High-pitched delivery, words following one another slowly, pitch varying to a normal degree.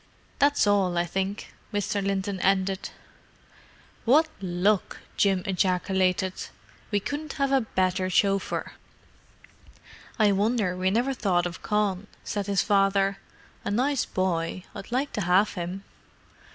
No: high, 195 Hz; slow, 125 wpm; narrow, 2.1 semitones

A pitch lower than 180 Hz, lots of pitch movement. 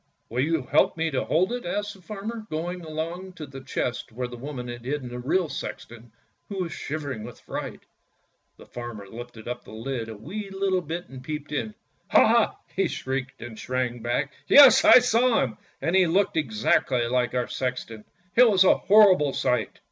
Yes: medium, 140 Hz; wide, 7.1 semitones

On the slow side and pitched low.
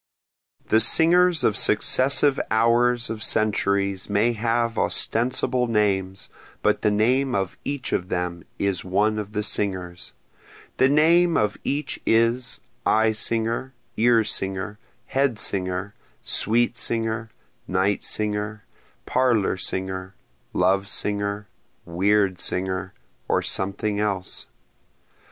Yes: slow, 110 wpm; low, 105 Hz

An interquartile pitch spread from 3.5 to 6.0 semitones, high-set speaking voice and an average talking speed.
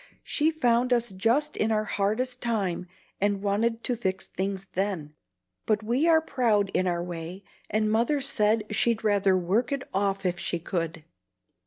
Yes: average, 3.9 semitones; high, 210 Hz; average, 165 wpm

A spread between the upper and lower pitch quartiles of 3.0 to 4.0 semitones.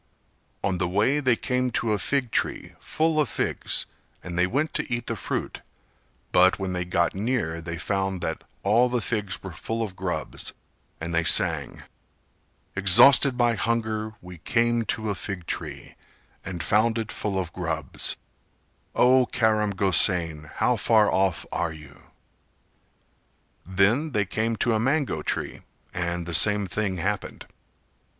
No: average, 4.6 semitones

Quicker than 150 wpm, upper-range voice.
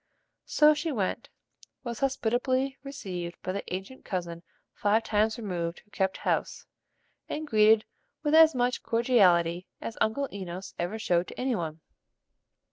No: average, 140 wpm; high, 215 Hz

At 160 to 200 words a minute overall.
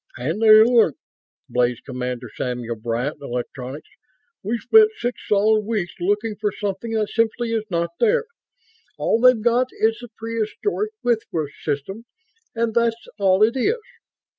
No: average, 140 wpm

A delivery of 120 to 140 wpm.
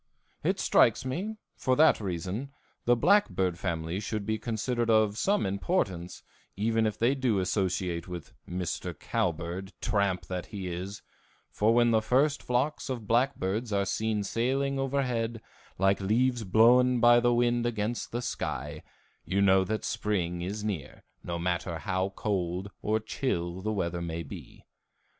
No: average, 150 wpm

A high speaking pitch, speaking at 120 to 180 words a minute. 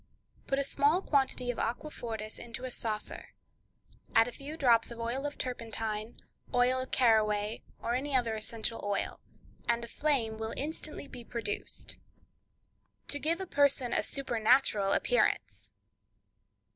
Yes: high, 240 Hz; average, 140 wpm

